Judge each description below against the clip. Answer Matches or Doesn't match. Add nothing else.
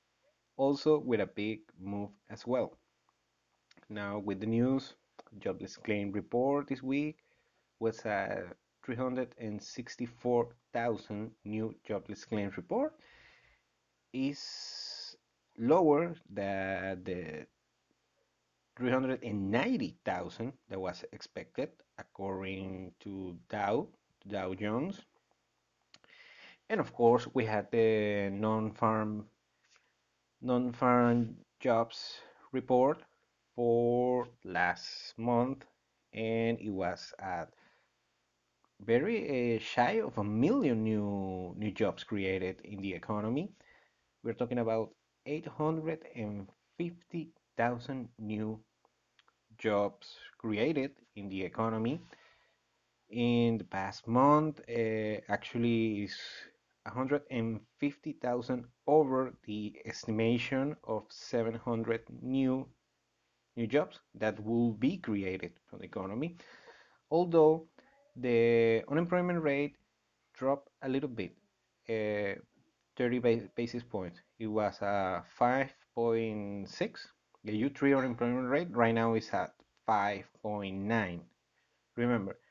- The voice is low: Matches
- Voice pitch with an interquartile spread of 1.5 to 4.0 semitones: Matches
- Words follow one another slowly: Matches